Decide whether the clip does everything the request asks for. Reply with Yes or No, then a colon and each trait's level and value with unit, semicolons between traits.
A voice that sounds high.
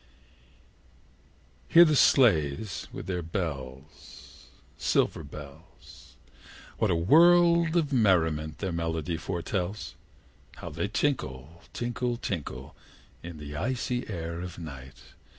No: very low, 85 Hz